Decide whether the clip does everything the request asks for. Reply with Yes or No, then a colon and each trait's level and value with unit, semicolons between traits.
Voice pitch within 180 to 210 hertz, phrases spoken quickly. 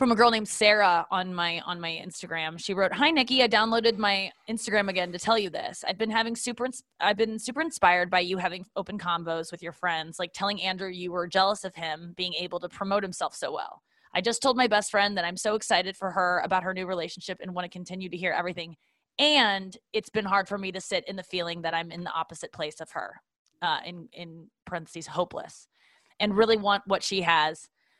Yes: high, 190 Hz; fast, 230 wpm